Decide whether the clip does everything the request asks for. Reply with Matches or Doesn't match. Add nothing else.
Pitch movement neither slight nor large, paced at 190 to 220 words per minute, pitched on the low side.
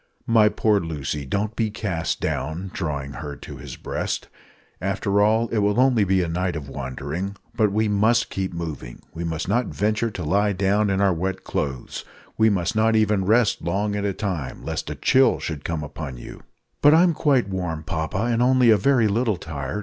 Matches